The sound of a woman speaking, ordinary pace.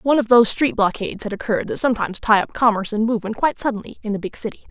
No: female; fast, 255 wpm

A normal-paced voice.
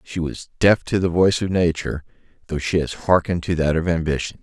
No: fast, 215 wpm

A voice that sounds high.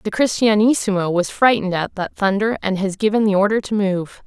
Yes: high, 200 Hz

